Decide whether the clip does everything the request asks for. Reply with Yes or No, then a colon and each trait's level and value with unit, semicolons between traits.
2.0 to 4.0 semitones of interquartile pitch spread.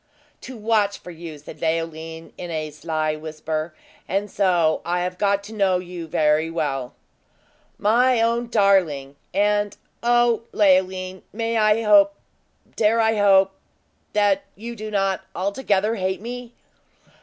No: average, 4.5 semitones